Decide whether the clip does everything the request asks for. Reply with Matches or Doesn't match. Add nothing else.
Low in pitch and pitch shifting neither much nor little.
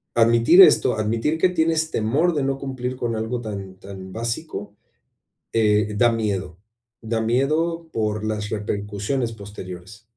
Matches